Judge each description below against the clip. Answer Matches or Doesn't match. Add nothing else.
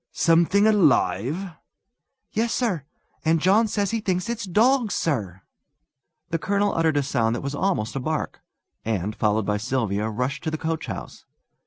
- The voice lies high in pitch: Doesn't match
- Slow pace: Doesn't match